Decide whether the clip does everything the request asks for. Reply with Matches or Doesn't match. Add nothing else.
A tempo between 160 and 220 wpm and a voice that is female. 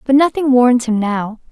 Matches